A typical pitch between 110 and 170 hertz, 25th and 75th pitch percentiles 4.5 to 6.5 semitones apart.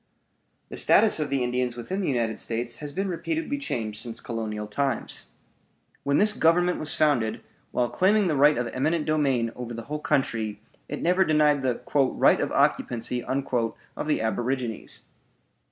Yes: low, 135 Hz; average, 4.8 semitones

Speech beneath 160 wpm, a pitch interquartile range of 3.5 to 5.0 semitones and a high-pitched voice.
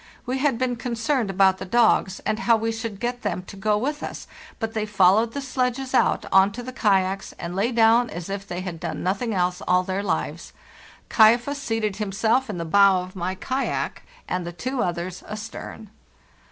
No: average, 200 wpm; average, 4.2 semitones; high, 215 Hz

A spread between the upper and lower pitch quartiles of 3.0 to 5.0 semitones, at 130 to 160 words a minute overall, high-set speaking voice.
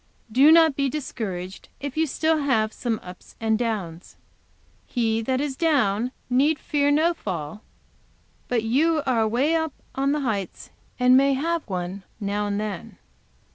No: wide, 5.4 semitones; average, 155 wpm; very high, 250 Hz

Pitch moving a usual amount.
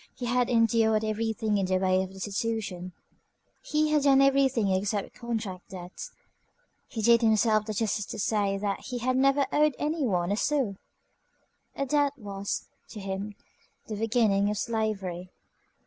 Yes: average, 3.9 semitones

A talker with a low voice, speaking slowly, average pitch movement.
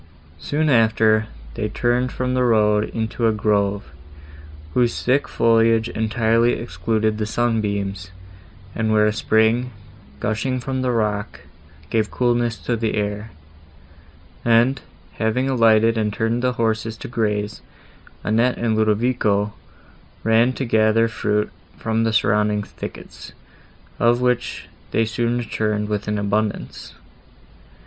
No: low, 110 Hz; slow, 125 wpm; narrow, 2.0 semitones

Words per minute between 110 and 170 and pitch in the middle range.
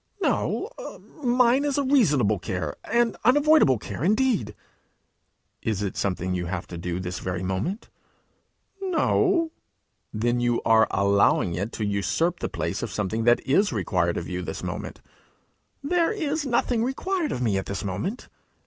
No: average, 155 wpm; low, 125 Hz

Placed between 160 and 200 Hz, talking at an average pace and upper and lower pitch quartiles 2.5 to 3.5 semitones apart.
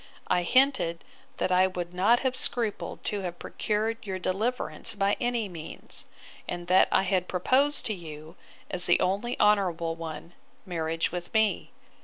No: medium, 185 Hz; average, 155 wpm; average, 4.0 semitones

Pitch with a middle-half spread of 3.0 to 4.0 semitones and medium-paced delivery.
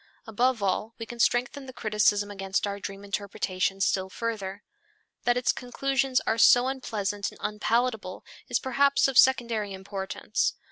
Yes: average, 3.7 semitones; average, 145 wpm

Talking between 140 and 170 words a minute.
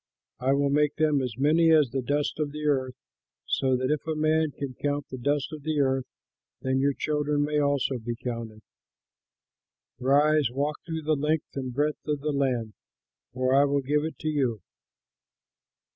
No: average, 180 wpm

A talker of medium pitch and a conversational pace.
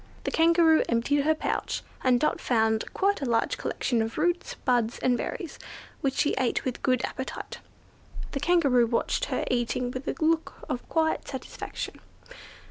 No: very high, 265 Hz; average, 165 wpm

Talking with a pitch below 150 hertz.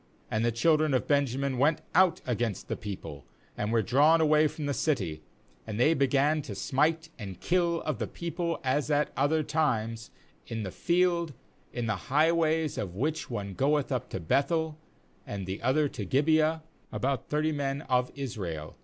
Yes: medium, 140 Hz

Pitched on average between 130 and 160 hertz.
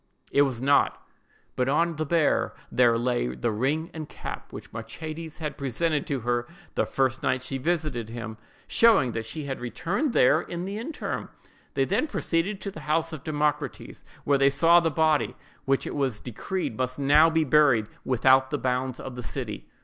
Yes: medium, 140 Hz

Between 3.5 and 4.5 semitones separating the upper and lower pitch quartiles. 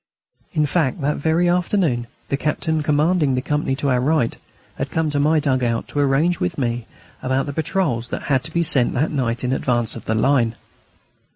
Yes: average, 4.1 semitones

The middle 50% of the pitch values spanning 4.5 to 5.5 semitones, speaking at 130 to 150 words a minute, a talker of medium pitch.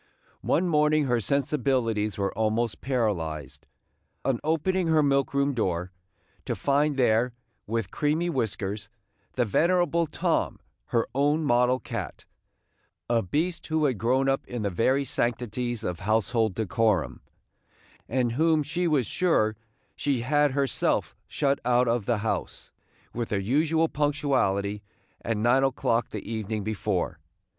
No: average, 5.0 semitones; slow, 135 wpm; low, 125 Hz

